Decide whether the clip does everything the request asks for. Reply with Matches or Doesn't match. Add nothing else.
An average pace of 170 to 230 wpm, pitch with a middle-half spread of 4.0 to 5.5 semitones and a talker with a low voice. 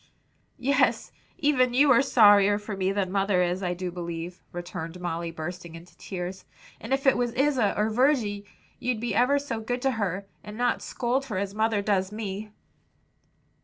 Doesn't match